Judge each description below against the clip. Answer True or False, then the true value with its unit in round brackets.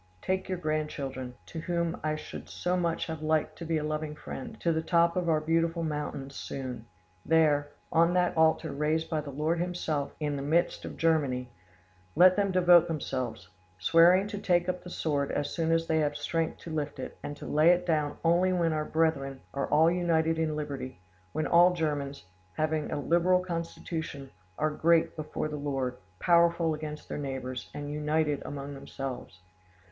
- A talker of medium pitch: True (155 Hz)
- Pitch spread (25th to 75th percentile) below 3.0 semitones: True (2.6 semitones)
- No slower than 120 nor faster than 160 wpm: False (180 wpm)